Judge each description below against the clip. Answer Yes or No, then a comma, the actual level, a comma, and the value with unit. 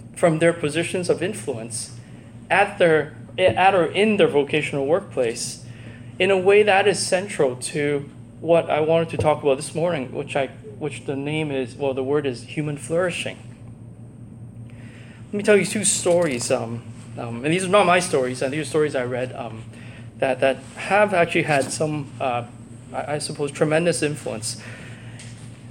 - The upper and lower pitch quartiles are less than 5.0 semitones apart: No, wide, 5.4 semitones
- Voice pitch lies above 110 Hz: Yes, low, 135 Hz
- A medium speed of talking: Yes, average, 170 wpm